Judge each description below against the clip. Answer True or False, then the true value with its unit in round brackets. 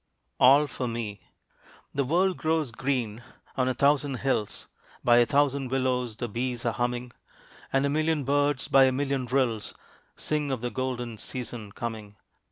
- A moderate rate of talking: True (160 wpm)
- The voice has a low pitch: True (130 Hz)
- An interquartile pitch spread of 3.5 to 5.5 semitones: False (2.8 semitones)